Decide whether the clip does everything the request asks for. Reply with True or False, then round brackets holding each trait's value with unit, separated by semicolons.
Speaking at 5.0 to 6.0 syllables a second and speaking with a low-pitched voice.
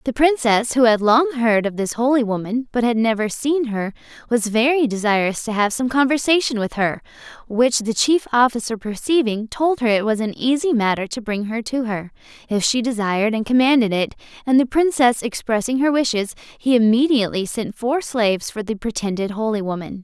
False (5.3 syllables/s; 235 Hz)